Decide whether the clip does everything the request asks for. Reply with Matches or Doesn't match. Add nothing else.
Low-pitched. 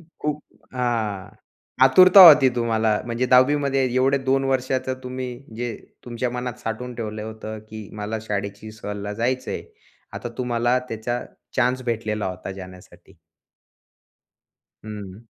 Matches